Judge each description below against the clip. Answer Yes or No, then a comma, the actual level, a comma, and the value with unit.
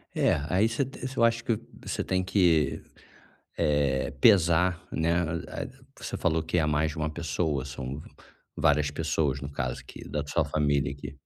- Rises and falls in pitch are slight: No, average, 3.7 semitones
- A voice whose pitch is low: Yes, very low, 80 Hz